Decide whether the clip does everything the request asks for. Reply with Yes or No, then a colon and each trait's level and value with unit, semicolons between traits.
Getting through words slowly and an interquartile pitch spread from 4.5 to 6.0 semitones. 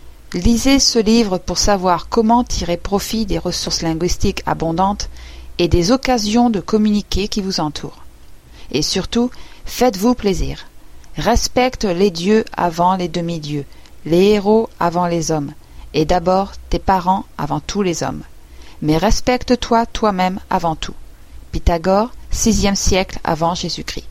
Yes: slow, 130 wpm; average, 4.9 semitones